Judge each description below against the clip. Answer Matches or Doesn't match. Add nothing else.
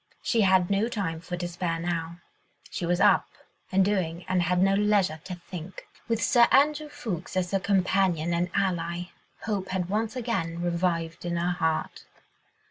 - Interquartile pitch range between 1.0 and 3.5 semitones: Matches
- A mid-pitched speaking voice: Matches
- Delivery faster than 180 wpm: Doesn't match